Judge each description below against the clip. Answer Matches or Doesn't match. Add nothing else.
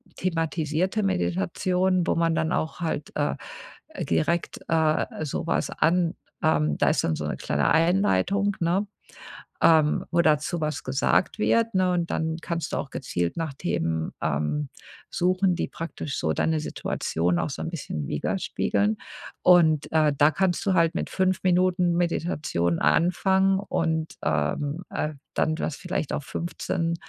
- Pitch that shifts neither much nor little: Matches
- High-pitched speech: Doesn't match